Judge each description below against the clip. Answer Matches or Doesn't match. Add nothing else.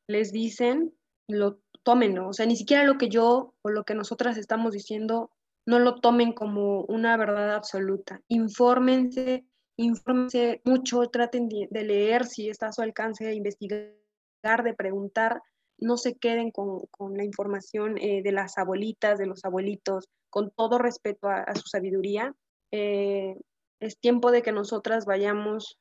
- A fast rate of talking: Doesn't match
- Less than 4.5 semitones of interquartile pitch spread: Matches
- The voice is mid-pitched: Doesn't match